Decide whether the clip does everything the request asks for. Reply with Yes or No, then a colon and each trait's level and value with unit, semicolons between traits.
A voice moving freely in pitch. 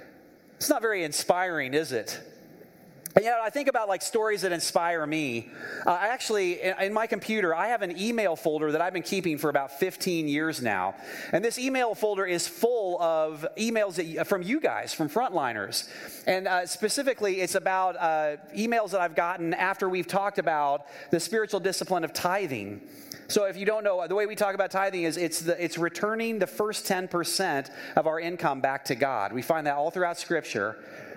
No: average, 4.2 semitones